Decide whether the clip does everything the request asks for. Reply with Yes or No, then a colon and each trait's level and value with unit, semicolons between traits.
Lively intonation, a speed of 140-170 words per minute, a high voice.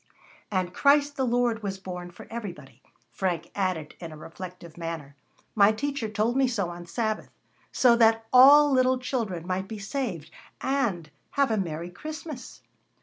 Yes: wide, 6.4 semitones; average, 155 wpm; high, 210 Hz